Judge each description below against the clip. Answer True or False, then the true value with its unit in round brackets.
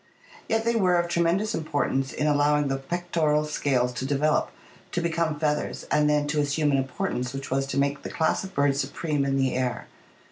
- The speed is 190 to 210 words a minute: True (205 wpm)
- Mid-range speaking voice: True (150 Hz)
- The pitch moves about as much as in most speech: True (3.5 semitones)